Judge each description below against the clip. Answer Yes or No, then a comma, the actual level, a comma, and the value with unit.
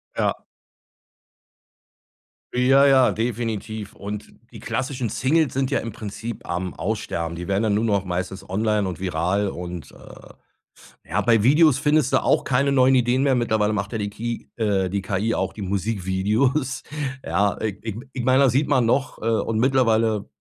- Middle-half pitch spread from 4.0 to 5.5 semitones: Yes, average, 4.4 semitones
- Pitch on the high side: No, low, 110 Hz